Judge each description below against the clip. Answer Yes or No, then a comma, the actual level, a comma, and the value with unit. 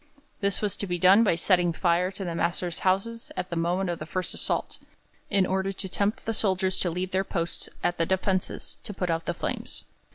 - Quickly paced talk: Yes, fast, 220 wpm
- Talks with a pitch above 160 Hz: Yes, medium, 185 Hz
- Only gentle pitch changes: Yes, narrow, 1.9 semitones